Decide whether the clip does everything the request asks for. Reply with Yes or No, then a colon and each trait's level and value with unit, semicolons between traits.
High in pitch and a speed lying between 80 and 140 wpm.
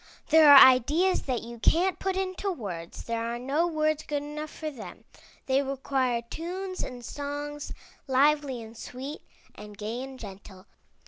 No: very high, 275 Hz; average, 155 wpm